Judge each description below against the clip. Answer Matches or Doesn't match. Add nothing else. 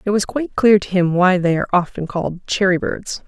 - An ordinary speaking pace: Doesn't match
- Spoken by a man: Doesn't match